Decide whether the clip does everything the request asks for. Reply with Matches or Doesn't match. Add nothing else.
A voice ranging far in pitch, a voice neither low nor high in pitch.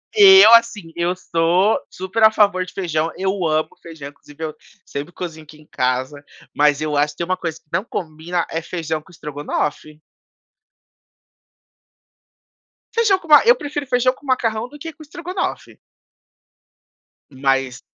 Matches